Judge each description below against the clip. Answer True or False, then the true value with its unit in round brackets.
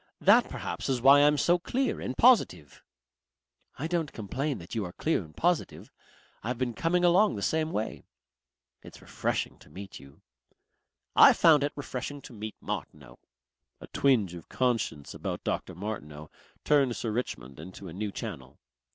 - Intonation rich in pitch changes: True (8.7 semitones)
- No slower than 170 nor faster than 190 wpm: False (160 wpm)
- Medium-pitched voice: False (120 Hz)